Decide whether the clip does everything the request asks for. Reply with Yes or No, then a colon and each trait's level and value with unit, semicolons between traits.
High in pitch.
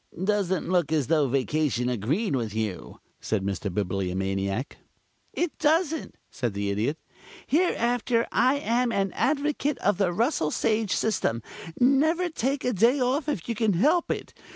Yes: high, 200 Hz